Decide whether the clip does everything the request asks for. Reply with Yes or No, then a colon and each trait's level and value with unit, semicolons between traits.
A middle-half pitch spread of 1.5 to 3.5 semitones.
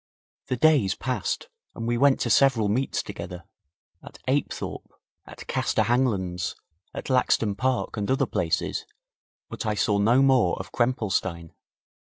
No: average, 4.5 semitones